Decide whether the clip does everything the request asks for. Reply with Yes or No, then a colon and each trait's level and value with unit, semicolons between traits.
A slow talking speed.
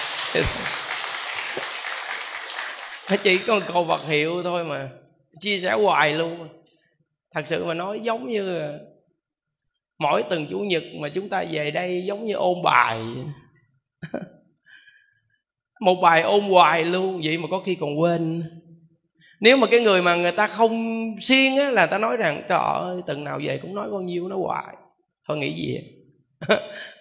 Yes: slow, 160 wpm